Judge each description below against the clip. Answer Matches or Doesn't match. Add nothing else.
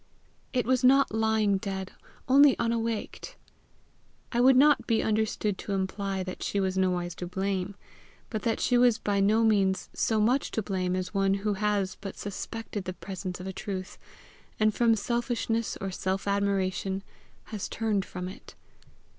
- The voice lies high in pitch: Matches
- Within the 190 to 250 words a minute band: Doesn't match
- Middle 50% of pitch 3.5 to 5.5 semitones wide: Doesn't match